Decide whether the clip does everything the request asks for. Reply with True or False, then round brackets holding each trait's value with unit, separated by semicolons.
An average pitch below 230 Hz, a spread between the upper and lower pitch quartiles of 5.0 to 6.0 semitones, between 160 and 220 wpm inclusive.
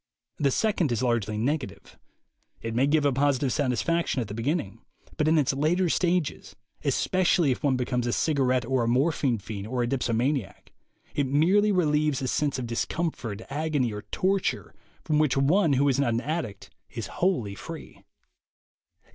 False (135 Hz; 4.4 semitones; 165 wpm)